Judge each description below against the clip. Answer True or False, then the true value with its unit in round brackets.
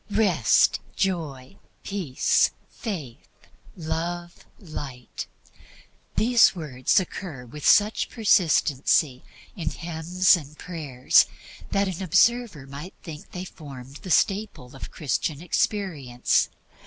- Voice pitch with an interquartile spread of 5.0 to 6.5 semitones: True (5.4 semitones)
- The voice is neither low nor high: True (165 Hz)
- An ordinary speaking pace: False (100 wpm)